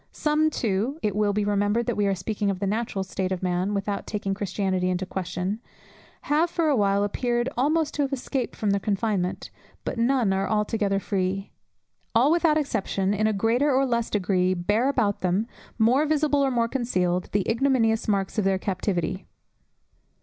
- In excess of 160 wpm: Yes, average, 180 wpm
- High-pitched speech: Yes, high, 210 Hz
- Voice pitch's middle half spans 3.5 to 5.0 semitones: Yes, average, 4.3 semitones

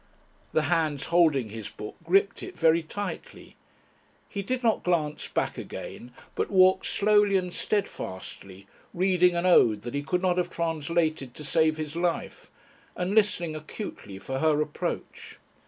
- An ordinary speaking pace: Yes, average, 150 wpm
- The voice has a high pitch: No, medium, 165 Hz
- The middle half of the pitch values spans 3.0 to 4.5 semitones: Yes, average, 3.8 semitones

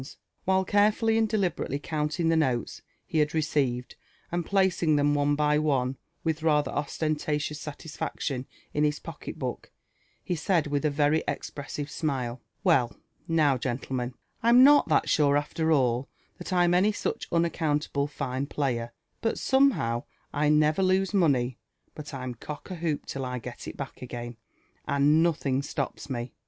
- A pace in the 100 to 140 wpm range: No, average, 155 wpm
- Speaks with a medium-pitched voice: Yes, medium, 150 Hz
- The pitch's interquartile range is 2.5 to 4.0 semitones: Yes, average, 3.6 semitones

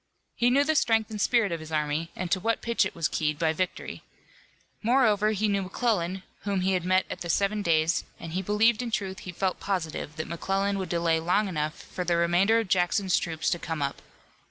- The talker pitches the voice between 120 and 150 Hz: No, medium, 185 Hz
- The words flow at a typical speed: No, fast, 225 wpm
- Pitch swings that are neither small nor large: Yes, average, 3.9 semitones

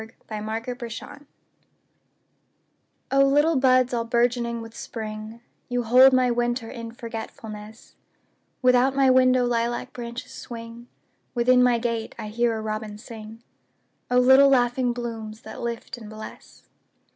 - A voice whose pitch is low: No, high, 235 Hz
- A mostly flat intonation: Yes, narrow, 1.8 semitones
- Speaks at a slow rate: Yes, slow, 120 wpm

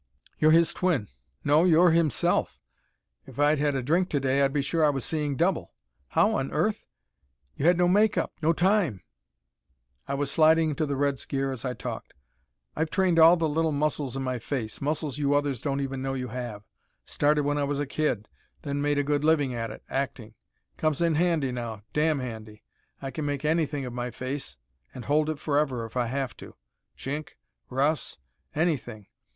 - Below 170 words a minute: No, average, 195 wpm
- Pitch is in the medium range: Yes, medium, 145 Hz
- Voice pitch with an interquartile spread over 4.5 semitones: No, average, 3.2 semitones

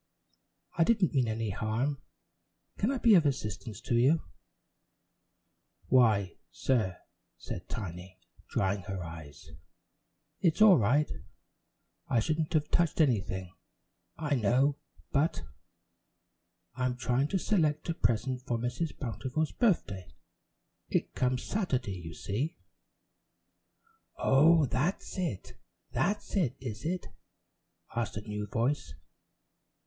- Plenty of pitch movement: Yes, wide, 6.8 semitones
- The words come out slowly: Yes, slow, 115 wpm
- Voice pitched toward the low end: Yes, low, 125 Hz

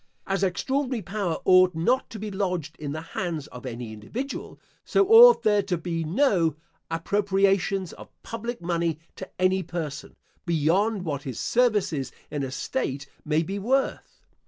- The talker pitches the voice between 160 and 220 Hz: Yes, medium, 185 Hz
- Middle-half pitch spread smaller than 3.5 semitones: No, average, 4.7 semitones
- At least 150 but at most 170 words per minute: Yes, average, 155 wpm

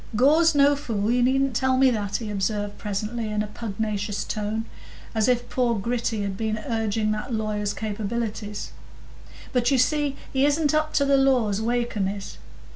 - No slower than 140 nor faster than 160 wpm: No, average, 175 wpm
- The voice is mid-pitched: No, high, 225 Hz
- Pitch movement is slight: No, average, 3.8 semitones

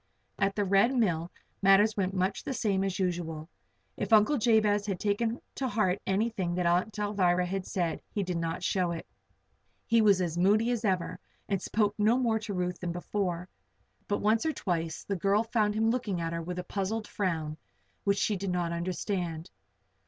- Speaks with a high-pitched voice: Yes, high, 195 Hz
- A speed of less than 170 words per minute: No, average, 190 wpm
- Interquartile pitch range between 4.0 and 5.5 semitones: No, average, 3.2 semitones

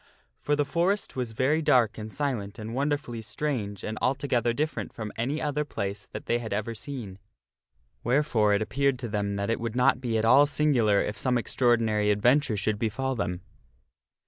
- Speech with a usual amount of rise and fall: Yes, average, 4.5 semitones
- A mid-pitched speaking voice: No, low, 120 Hz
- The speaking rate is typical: Yes, average, 180 wpm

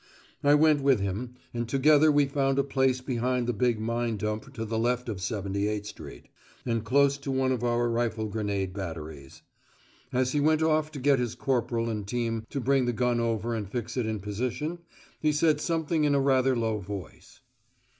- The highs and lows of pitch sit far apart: No, average, 4.0 semitones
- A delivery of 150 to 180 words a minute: No, average, 195 wpm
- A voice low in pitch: Yes, low, 120 Hz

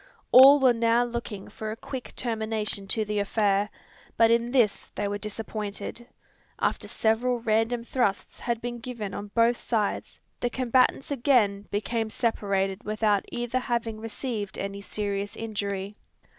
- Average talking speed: Yes, average, 145 wpm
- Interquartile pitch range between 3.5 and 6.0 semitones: No, average, 2.7 semitones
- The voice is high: Yes, high, 225 Hz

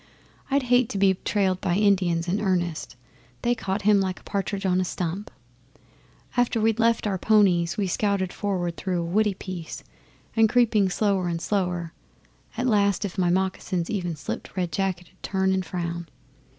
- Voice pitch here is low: No, high, 190 Hz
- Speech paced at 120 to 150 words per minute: No, average, 175 wpm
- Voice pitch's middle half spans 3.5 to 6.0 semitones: No, average, 2.8 semitones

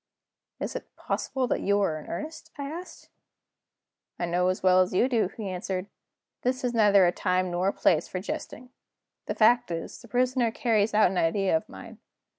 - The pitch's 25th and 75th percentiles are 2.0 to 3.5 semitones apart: No, average, 5.0 semitones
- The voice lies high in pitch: Yes, high, 200 Hz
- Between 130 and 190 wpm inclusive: No, average, 200 wpm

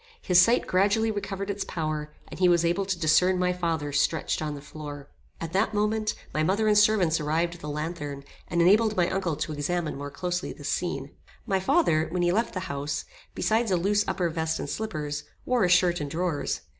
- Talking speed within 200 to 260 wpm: Yes, fast, 205 wpm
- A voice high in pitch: No, medium, 175 Hz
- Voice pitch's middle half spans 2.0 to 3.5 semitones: No, average, 4.1 semitones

